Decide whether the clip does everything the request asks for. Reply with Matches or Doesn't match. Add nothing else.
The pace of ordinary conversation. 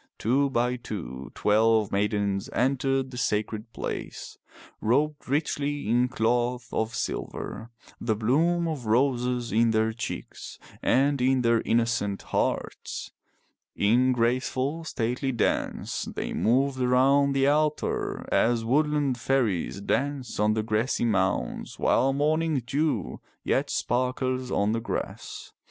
Doesn't match